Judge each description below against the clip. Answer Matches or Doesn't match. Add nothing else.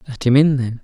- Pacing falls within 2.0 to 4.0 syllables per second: Doesn't match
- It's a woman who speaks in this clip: Doesn't match